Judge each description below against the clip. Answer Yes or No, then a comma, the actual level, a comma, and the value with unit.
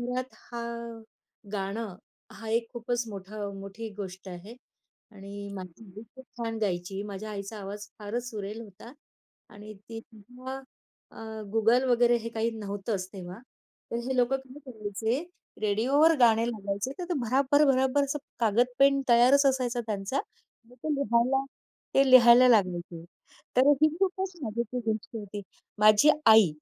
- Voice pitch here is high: Yes, high, 225 Hz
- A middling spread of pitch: Yes, average, 3.7 semitones